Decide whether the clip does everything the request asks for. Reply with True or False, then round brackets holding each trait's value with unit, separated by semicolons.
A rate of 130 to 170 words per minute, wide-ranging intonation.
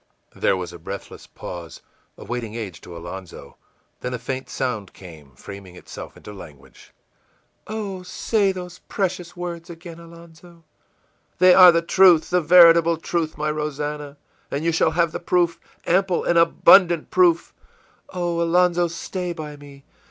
True (150 wpm; 5.9 semitones)